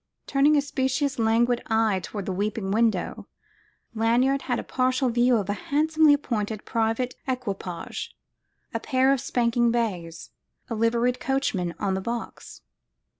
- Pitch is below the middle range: No, high, 235 Hz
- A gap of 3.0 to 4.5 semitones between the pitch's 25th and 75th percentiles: Yes, average, 3.4 semitones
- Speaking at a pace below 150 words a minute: Yes, average, 140 wpm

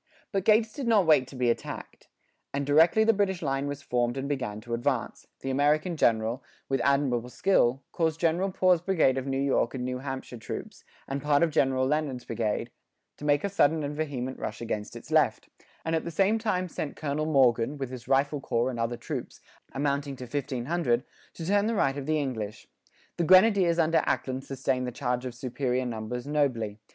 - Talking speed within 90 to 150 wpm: No, average, 195 wpm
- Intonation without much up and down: No, average, 4.4 semitones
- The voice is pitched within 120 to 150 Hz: Yes, medium, 140 Hz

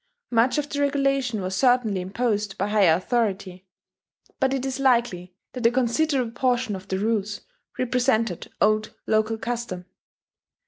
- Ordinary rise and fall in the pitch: Yes, average, 4.1 semitones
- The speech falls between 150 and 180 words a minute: No, average, 140 wpm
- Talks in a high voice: Yes, high, 230 Hz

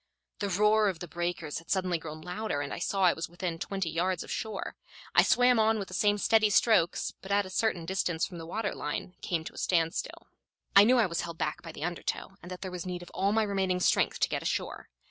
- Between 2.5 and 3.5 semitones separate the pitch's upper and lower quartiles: Yes, average, 3.2 semitones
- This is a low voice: No, medium, 185 Hz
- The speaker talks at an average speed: No, fast, 245 wpm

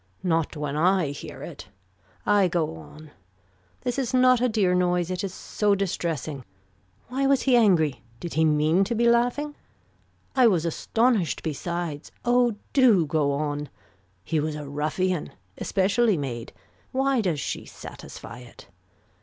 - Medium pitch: Yes, medium, 180 Hz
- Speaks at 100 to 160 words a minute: Yes, average, 145 wpm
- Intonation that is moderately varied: No, wide, 7.5 semitones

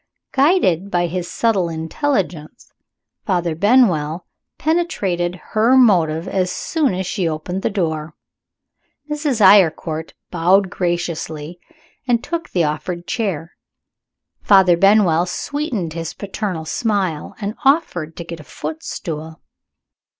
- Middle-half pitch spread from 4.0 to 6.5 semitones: Yes, average, 4.7 semitones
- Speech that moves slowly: Yes, slow, 115 wpm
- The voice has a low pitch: No, medium, 180 Hz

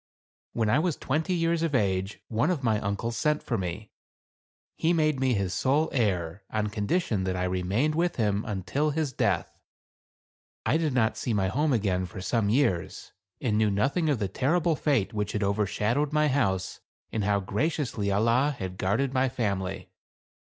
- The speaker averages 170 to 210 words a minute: Yes, average, 175 wpm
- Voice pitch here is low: Yes, low, 115 Hz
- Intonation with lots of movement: Yes, wide, 6.7 semitones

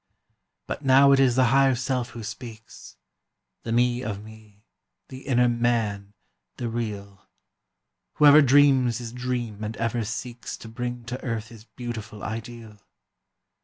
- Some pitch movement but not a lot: No, narrow, 2.3 semitones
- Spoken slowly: Yes, slow, 130 wpm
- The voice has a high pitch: No, low, 120 Hz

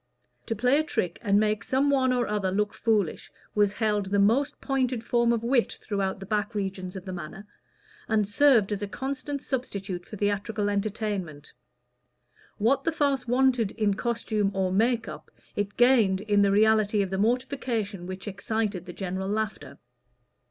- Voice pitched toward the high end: Yes, high, 210 Hz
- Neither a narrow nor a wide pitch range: Yes, average, 3.5 semitones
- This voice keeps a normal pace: Yes, average, 170 wpm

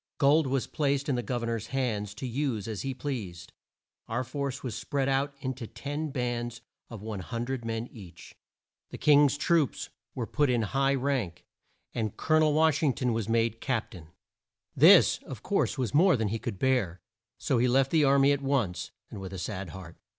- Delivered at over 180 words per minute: Yes, average, 200 wpm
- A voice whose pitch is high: No, low, 125 Hz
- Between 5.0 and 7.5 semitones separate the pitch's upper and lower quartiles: No, average, 3.9 semitones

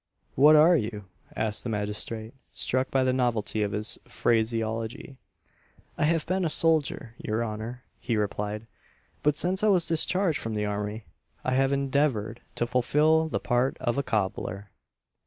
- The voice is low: Yes, low, 120 Hz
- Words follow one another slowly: No, average, 155 wpm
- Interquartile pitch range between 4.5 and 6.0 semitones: Yes, wide, 5.5 semitones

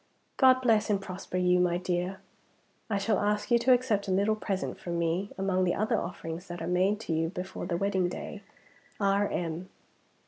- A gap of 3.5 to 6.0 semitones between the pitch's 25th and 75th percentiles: No, average, 2.7 semitones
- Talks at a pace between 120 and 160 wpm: No, average, 185 wpm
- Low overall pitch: No, high, 190 Hz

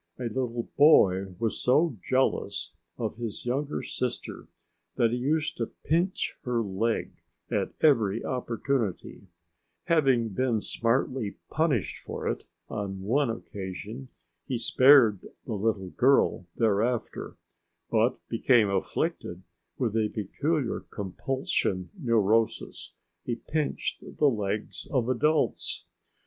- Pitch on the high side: No, low, 120 Hz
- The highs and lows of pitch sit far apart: No, average, 4.1 semitones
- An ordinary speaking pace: No, slow, 110 wpm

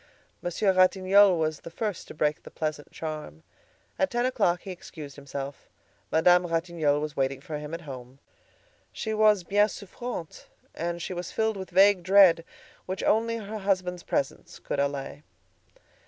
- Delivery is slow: No, average, 155 wpm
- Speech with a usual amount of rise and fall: Yes, average, 4.7 semitones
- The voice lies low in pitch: No, medium, 175 Hz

